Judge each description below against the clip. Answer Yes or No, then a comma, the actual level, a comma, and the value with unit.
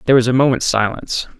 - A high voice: No, low, 125 Hz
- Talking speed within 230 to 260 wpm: No, fast, 215 wpm